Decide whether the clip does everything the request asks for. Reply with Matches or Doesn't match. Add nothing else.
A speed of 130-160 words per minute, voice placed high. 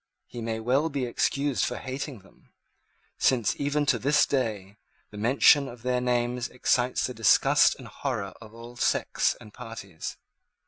Doesn't match